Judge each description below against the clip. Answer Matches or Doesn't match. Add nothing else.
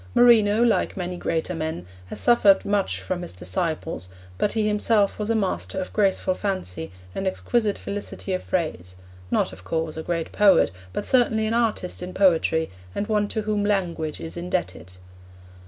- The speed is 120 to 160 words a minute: Doesn't match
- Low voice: Doesn't match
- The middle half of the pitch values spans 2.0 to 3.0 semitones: Doesn't match